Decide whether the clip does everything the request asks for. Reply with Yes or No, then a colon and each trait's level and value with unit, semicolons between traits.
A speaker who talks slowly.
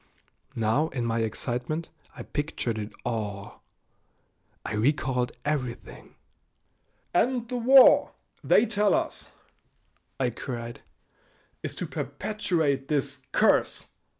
Yes: slow, 100 wpm